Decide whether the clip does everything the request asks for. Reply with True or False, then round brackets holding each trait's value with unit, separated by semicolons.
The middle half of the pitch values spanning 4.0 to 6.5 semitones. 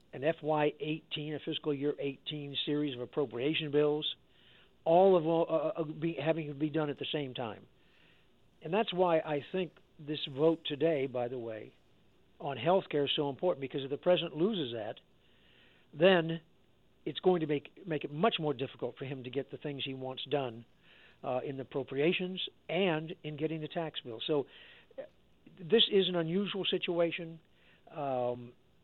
False (3.2 semitones)